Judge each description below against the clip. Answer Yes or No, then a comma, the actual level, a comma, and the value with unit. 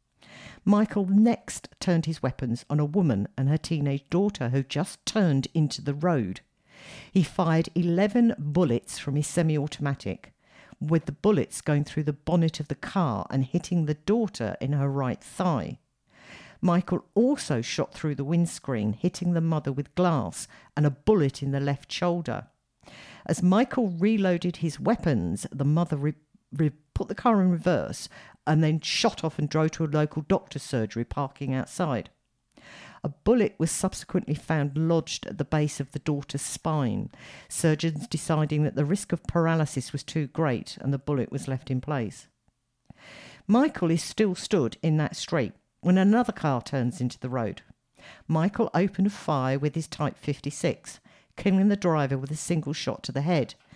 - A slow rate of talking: No, average, 165 wpm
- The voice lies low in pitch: No, medium, 155 Hz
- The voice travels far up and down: No, average, 4.1 semitones